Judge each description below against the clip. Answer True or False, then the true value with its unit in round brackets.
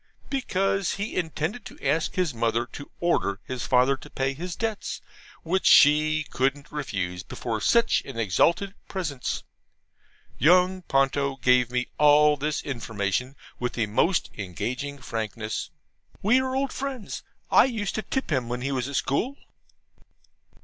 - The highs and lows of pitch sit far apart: True (6.8 semitones)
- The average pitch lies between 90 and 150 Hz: True (140 Hz)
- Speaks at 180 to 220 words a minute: False (145 wpm)